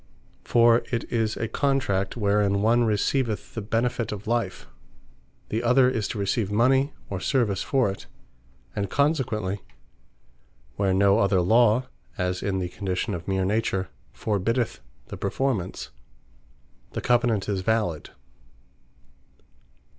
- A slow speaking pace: Yes, slow, 125 wpm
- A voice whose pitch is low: Yes, low, 105 Hz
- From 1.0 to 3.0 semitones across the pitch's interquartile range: No, average, 3.5 semitones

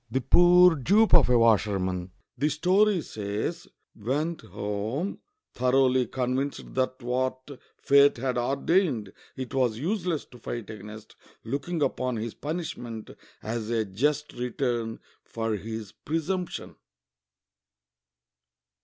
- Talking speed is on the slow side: Yes, slow, 120 wpm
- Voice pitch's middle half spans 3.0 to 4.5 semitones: No, average, 5.1 semitones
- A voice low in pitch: Yes, low, 130 Hz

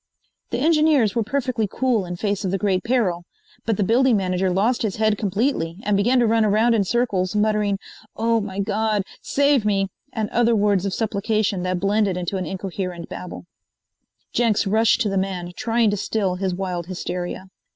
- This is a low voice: No, high, 205 Hz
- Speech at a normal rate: Yes, average, 180 wpm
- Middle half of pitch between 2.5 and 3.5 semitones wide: Yes, average, 3.2 semitones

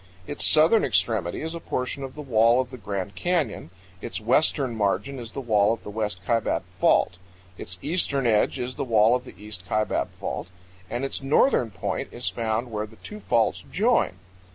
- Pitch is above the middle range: No, low, 115 Hz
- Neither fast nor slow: Yes, average, 190 wpm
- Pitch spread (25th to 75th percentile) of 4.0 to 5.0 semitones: Yes, average, 4.4 semitones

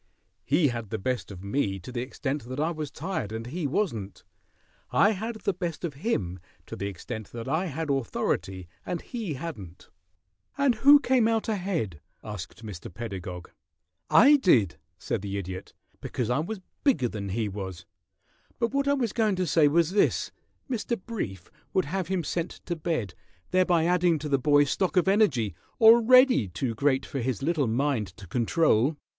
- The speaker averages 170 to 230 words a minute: Yes, average, 180 wpm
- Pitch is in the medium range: Yes, medium, 145 Hz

